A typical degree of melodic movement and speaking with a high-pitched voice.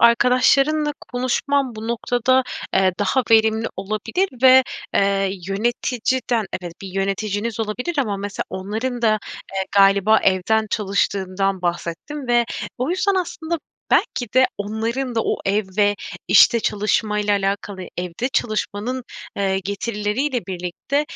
Yes: average, 4.2 semitones; high, 215 Hz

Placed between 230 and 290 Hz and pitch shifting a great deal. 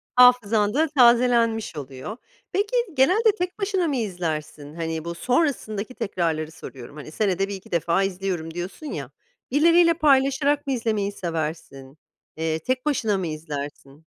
No: high, 205 Hz; wide, 8.6 semitones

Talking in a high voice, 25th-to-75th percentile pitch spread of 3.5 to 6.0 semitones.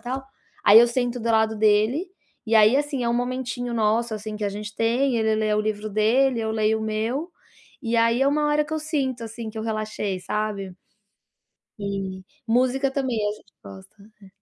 No: high, 225 Hz; average, 3.0 semitones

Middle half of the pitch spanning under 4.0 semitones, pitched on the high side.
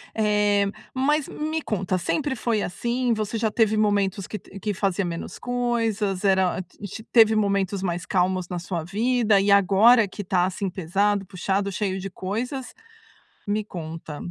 Yes: average, 2.9 semitones; high, 200 Hz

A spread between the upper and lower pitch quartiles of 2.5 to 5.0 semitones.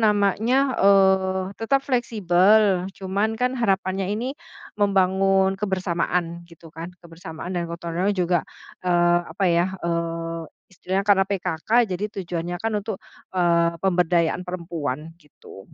Yes: average, 2.8 semitones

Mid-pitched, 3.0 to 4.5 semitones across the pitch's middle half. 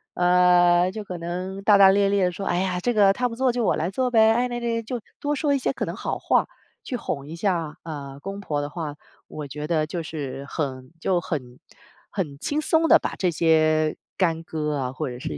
No: medium, 175 Hz; average, 5.3 semitones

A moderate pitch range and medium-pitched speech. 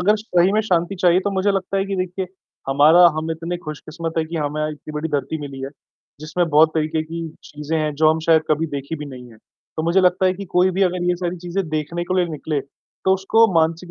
Yes: average, 3.1 semitones; medium, 165 Hz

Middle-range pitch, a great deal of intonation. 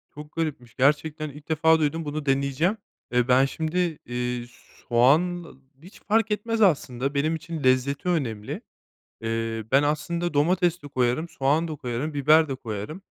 No: medium, 150 Hz; average, 4.1 semitones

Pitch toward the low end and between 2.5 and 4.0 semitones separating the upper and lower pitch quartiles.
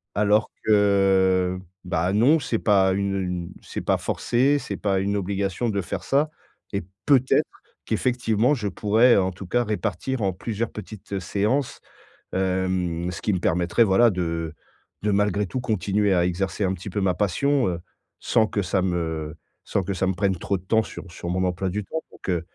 Yes: low, 100 Hz; average, 3.0 semitones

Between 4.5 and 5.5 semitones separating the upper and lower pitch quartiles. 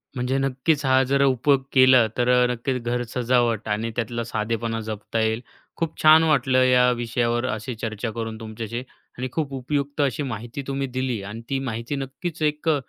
No: average, 2.9 semitones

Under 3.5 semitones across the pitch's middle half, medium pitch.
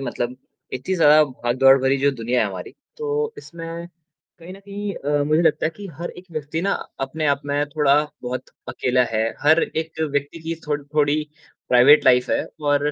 No: average, 3.9 semitones; medium, 145 Hz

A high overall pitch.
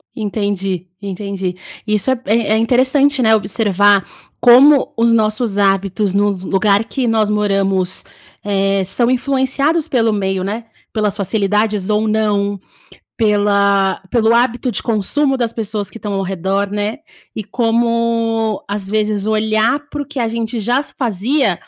Yes: high, 215 Hz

